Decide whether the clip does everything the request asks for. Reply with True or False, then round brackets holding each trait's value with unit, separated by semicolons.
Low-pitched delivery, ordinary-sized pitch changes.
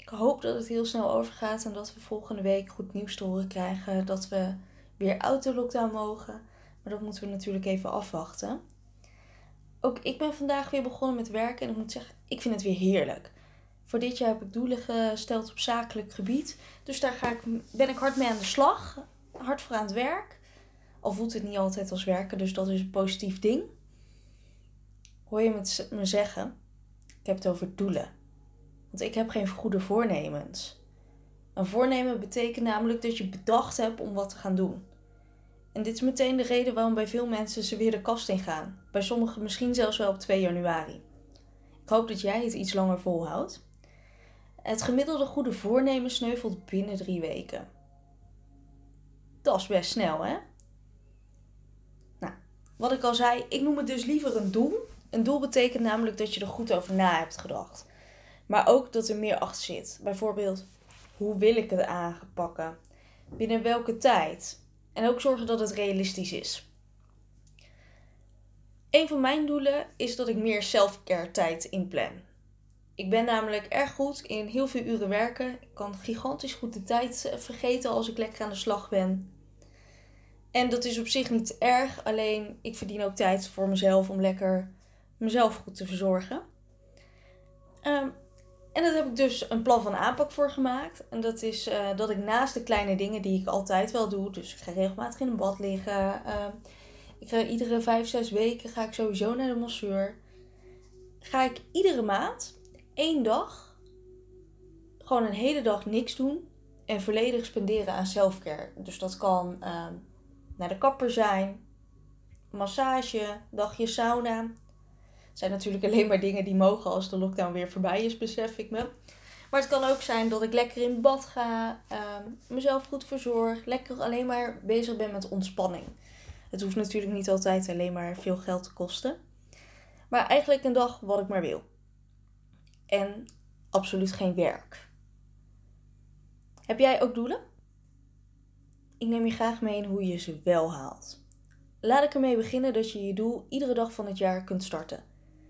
False (210 Hz; 4.4 semitones)